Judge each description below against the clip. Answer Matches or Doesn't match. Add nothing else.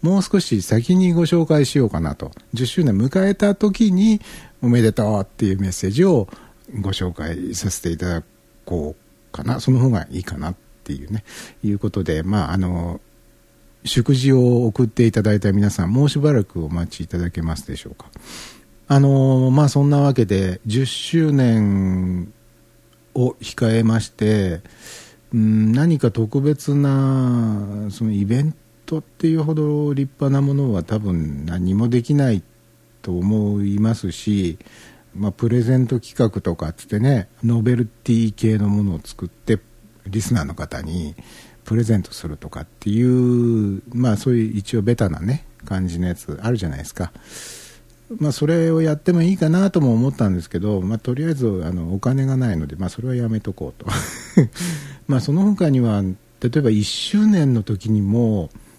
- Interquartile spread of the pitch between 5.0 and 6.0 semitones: Matches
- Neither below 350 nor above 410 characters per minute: Doesn't match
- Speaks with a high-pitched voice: Doesn't match